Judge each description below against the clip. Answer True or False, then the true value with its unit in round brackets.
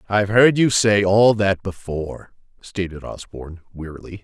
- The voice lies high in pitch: False (100 Hz)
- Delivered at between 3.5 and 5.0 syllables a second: True (4.9 syllables/s)